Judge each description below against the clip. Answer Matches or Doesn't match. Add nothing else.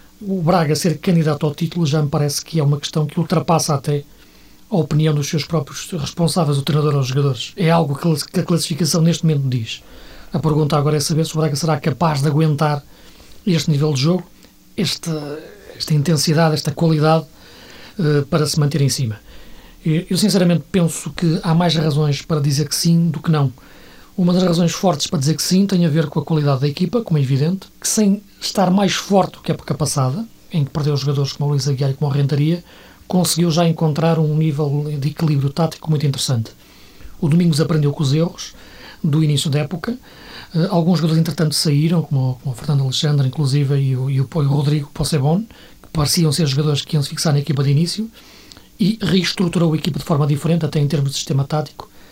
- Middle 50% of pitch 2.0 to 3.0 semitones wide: Matches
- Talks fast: Matches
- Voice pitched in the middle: Matches